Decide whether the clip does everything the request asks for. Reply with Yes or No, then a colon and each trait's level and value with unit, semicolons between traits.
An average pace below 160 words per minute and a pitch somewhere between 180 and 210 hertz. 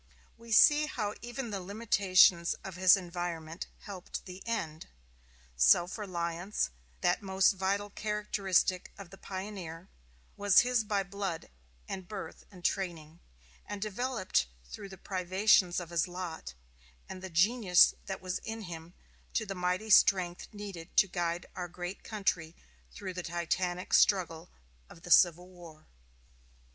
Yes: average, 140 wpm; medium, 185 Hz